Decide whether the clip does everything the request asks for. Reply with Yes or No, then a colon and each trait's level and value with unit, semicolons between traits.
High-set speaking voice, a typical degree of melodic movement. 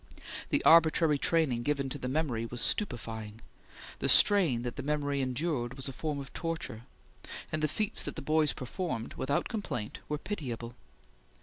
No: medium, 140 Hz; average, 4.6 semitones